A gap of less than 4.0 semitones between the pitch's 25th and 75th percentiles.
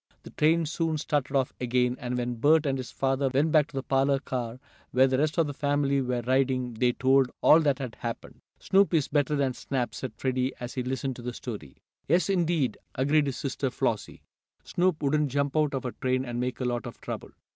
Yes: average, 2.7 semitones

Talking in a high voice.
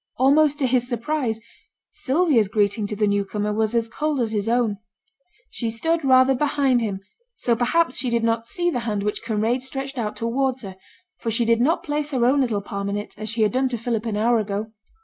Yes: high, 235 Hz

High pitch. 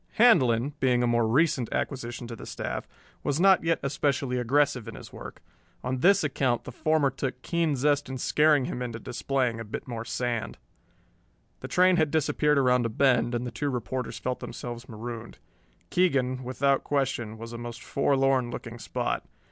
No: low, 130 Hz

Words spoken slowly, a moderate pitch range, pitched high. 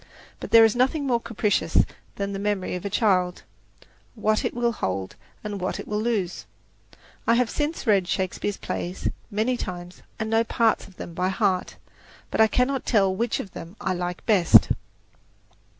No: average, 175 wpm; average, 3.9 semitones; high, 205 Hz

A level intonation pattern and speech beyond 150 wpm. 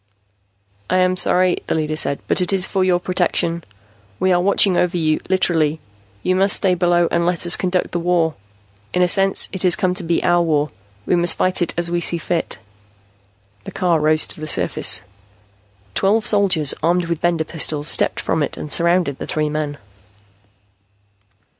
Yes: narrow, 2.3 semitones; average, 185 wpm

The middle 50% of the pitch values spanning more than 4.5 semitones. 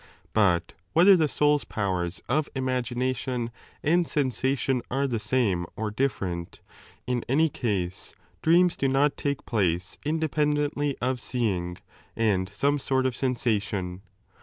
Yes: wide, 5.5 semitones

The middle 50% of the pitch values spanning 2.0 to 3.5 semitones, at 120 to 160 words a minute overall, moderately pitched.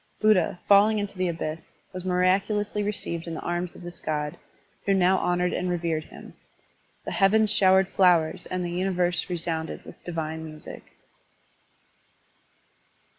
Yes: narrow, 2.6 semitones; average, 140 wpm; medium, 180 Hz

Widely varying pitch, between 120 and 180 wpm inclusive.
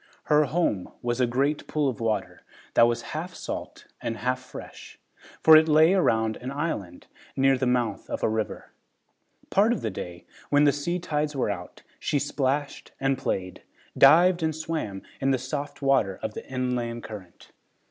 No: average, 4.6 semitones; average, 175 wpm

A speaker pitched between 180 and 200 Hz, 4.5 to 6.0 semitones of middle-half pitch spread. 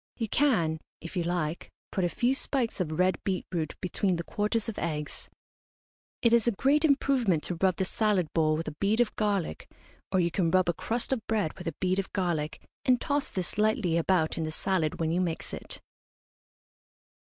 Yes: medium, 185 Hz; average, 4.8 semitones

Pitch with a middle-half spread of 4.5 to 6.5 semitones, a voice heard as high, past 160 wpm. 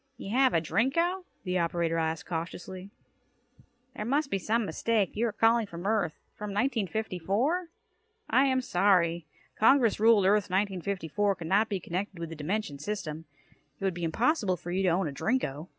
Yes: average, 4.8 semitones; high, 195 Hz; average, 170 wpm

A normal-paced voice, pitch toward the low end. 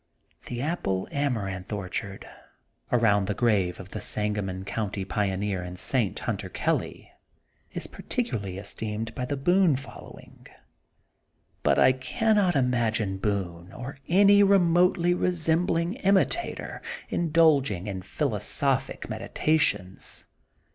No: slow, 115 wpm; low, 115 Hz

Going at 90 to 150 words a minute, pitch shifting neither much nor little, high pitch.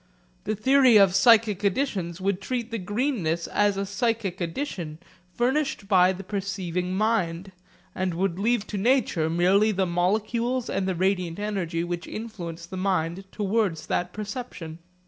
Yes: average, 145 wpm; average, 3.5 semitones; high, 195 Hz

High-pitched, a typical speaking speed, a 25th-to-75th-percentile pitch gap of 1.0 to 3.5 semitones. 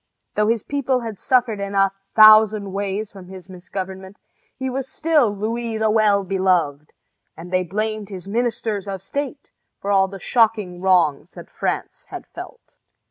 Yes: high, 205 Hz; average, 160 wpm; average, 2.9 semitones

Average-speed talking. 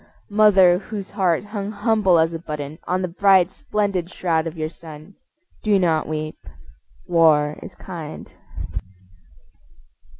No: slow, 130 wpm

